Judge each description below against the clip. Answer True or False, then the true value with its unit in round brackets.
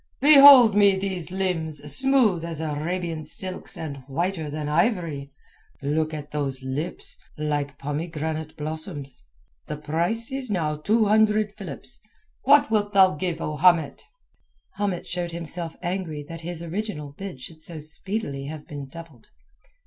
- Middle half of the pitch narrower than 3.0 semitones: False (4.4 semitones)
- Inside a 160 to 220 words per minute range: False (140 wpm)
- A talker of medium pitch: True (165 Hz)